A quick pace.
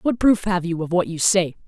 Yes: fast, 285 wpm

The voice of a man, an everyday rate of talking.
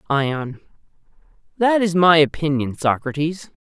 No: male; slow, 100 wpm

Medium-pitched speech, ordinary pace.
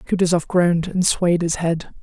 Yes: medium, 175 Hz; average, 180 wpm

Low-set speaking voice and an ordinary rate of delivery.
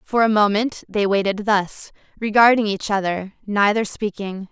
No: high, 205 Hz; average, 145 wpm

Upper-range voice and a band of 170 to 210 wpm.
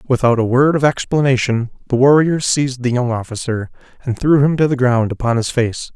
No: low, 130 Hz; average, 200 wpm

